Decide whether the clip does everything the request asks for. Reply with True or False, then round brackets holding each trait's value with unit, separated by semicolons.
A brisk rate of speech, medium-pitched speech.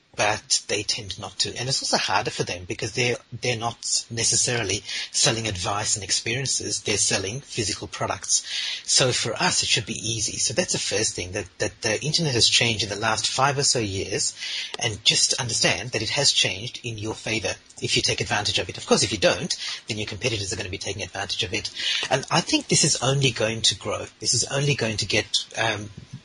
False (220 wpm; 115 Hz)